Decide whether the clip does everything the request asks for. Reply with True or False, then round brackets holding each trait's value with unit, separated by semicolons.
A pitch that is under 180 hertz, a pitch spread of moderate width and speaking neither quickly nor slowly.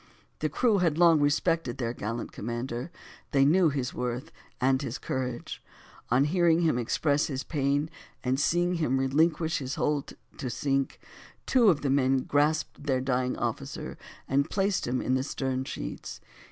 True (140 Hz; 3.7 semitones; 160 wpm)